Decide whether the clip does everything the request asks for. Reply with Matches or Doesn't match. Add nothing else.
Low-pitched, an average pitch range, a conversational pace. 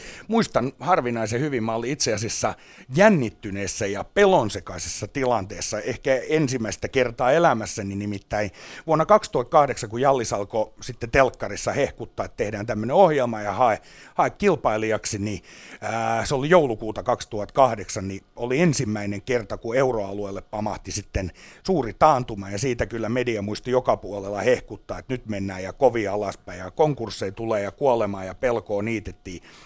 Matches